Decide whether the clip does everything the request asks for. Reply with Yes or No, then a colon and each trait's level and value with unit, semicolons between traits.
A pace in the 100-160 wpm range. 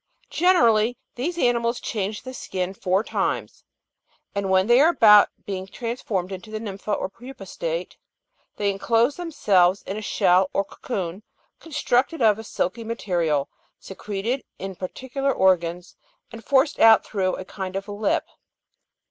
Yes: average, 145 wpm